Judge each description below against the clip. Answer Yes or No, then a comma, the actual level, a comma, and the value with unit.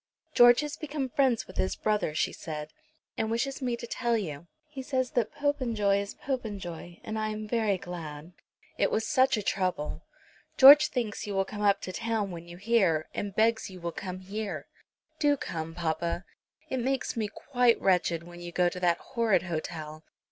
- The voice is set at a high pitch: Yes, high, 210 Hz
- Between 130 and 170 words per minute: No, average, 185 wpm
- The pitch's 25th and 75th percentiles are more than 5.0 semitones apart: Yes, wide, 5.5 semitones